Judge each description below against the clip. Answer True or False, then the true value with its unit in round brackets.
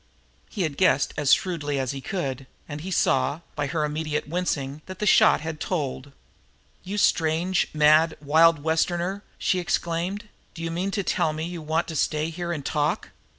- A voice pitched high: False (160 Hz)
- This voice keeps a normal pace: True (180 wpm)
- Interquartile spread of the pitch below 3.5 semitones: True (3.0 semitones)